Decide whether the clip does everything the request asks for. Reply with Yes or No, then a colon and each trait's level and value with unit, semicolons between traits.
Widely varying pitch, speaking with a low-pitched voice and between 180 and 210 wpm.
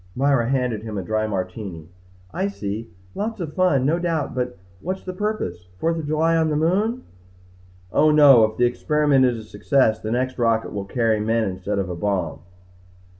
Yes: wide, 6.6 semitones; low, 125 Hz; average, 185 wpm